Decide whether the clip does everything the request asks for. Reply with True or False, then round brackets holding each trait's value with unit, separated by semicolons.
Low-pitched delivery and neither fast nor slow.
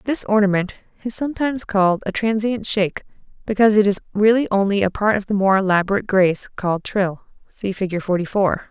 False (200 Hz; 180 wpm)